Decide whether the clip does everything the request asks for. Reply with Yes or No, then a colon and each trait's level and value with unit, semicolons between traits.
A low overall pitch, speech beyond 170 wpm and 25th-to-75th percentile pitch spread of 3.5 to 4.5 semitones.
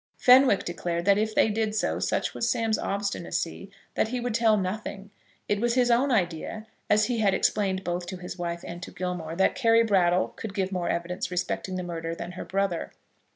No: high, 195 Hz; average, 200 wpm; average, 3.8 semitones